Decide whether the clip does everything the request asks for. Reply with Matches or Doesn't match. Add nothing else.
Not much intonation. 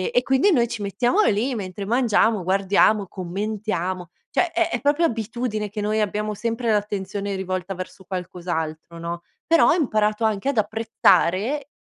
Doesn't match